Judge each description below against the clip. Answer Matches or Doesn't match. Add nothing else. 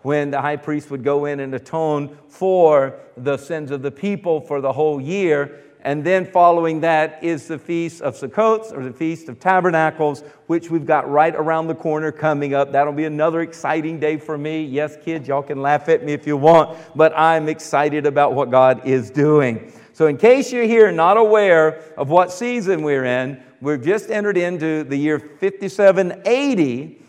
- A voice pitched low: Doesn't match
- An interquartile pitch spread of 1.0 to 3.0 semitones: Matches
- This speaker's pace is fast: Doesn't match